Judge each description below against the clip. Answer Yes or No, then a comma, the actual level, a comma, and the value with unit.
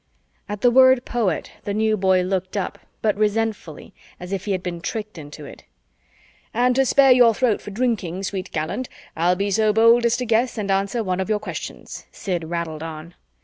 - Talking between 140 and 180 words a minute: No, average, 195 wpm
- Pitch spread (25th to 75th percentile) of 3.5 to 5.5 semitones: Yes, average, 4.1 semitones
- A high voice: Yes, high, 205 Hz